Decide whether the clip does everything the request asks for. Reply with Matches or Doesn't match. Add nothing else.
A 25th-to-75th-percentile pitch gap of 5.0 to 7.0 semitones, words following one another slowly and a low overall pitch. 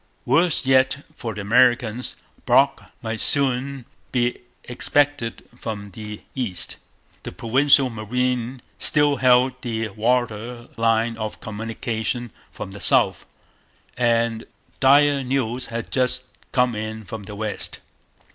Doesn't match